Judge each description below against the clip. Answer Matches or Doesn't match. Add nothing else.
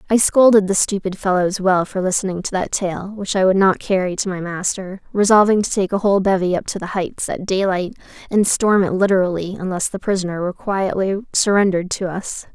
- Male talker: Doesn't match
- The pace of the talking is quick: Matches